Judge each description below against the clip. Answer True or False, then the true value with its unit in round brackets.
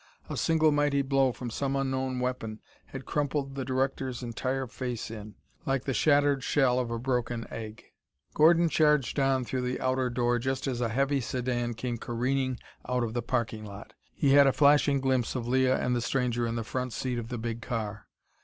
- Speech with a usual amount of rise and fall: False (2.3 semitones)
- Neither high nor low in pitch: False (130 Hz)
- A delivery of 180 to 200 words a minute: True (195 wpm)